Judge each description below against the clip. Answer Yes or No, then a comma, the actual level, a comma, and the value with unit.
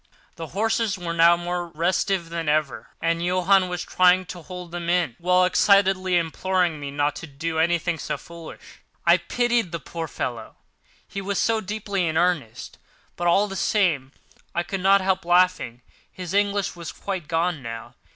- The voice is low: No, medium, 175 Hz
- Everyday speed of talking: Yes, average, 170 wpm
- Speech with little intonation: Yes, narrow, 2.3 semitones